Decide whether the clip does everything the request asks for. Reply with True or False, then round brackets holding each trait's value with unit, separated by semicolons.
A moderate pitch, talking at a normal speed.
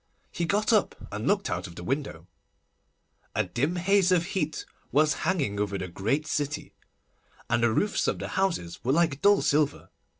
True (150 Hz; 175 wpm)